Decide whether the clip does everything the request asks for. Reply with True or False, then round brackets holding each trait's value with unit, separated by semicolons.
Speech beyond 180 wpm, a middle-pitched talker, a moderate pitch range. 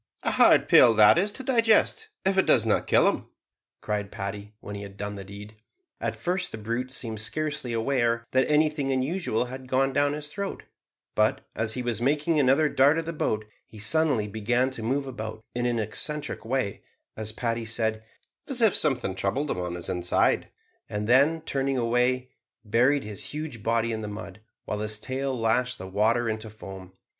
False (190 wpm; 120 Hz; 4.8 semitones)